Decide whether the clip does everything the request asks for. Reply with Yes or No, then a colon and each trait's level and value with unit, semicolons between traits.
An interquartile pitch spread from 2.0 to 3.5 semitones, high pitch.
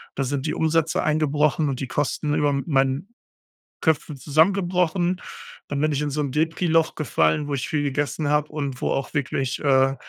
No: narrow, 2.4 semitones; medium, 150 Hz